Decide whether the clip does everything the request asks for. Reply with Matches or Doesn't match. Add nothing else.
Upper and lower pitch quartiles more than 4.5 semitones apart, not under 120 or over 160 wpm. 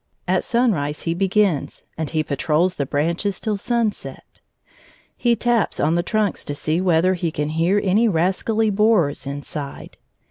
Matches